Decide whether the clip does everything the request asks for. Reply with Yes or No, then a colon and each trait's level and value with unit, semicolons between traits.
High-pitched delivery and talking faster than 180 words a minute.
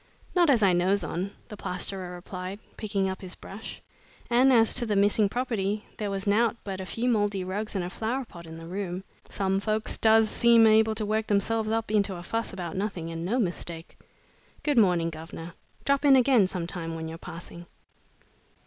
Yes: high, 200 Hz; average, 195 wpm